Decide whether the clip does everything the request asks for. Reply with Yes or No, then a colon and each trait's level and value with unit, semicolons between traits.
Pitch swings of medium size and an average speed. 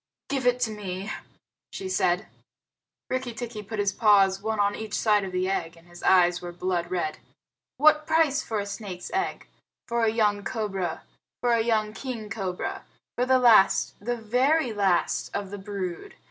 Yes: average, 3.9 semitones; average, 175 wpm